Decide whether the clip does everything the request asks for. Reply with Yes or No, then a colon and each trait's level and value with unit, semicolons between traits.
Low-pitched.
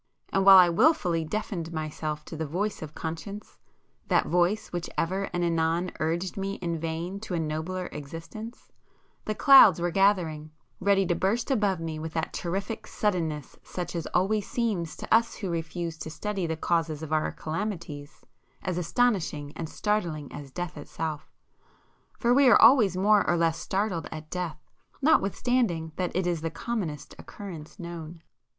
No: medium, 175 Hz